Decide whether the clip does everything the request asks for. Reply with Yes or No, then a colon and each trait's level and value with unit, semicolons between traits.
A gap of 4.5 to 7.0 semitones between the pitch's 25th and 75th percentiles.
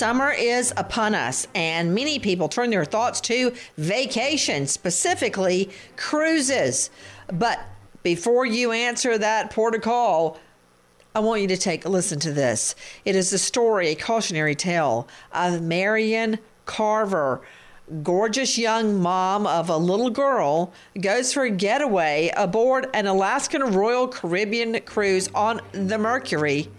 Yes: average, 5.0 semitones